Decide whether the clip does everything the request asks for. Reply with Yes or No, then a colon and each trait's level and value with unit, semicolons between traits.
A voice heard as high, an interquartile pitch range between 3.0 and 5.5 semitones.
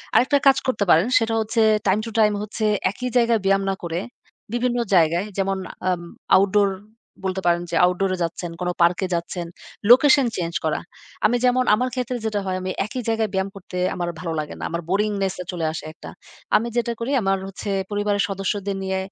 Yes: high, 195 Hz; average, 3.9 semitones